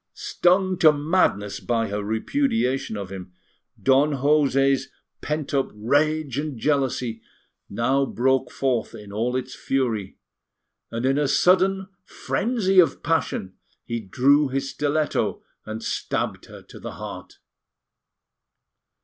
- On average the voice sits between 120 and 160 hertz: Yes, low, 135 Hz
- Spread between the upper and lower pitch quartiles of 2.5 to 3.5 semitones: No, average, 4.9 semitones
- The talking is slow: Yes, slow, 125 wpm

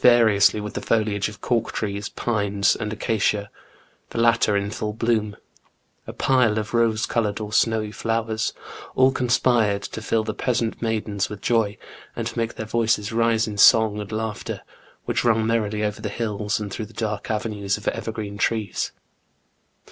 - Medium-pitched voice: No, low, 110 Hz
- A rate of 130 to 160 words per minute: No, average, 170 wpm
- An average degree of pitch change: No, narrow, 1.6 semitones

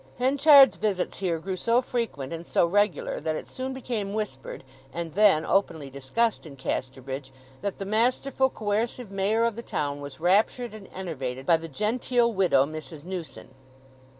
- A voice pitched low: No, high, 195 Hz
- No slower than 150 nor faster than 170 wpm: Yes, average, 160 wpm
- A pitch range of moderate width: No, wide, 6.7 semitones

